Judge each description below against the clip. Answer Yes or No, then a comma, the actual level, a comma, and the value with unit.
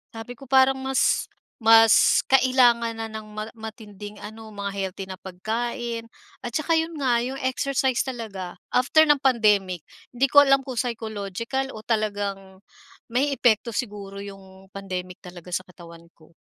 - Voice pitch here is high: Yes, high, 220 Hz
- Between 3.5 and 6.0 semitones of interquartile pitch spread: Yes, average, 4.5 semitones